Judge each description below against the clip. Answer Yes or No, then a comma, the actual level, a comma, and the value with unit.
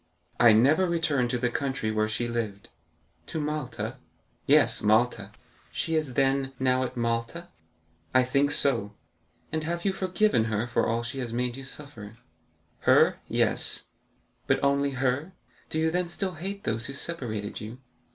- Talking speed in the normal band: Yes, average, 155 wpm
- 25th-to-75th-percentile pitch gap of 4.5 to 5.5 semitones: Yes, average, 5.0 semitones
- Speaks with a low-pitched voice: Yes, low, 130 Hz